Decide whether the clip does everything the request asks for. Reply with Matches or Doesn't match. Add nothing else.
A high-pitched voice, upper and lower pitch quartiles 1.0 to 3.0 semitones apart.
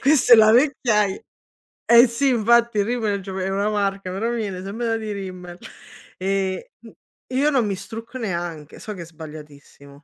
Doesn't match